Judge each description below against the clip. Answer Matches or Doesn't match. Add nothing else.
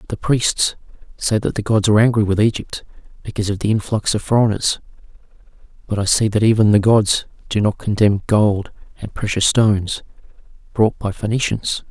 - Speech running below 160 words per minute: Doesn't match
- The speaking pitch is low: Matches